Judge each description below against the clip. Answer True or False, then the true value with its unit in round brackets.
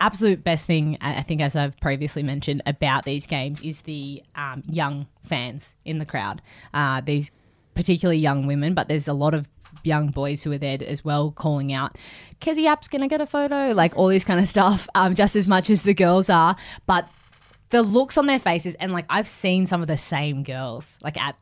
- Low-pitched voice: False (155 Hz)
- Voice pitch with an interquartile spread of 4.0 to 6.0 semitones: True (4.7 semitones)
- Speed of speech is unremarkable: False (215 wpm)